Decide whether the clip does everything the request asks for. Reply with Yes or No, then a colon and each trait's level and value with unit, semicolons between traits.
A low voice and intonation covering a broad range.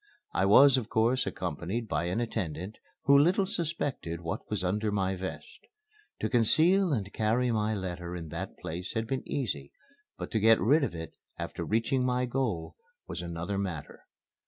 Yes: low, 110 Hz; wide, 6.0 semitones